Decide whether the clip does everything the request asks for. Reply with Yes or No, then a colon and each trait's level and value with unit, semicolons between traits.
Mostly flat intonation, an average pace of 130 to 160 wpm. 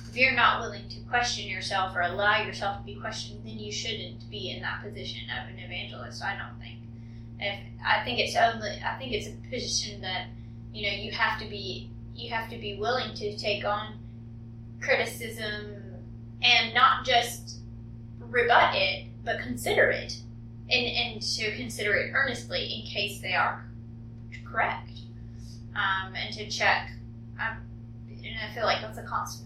No: narrow, 0.7 semitones; average, 170 wpm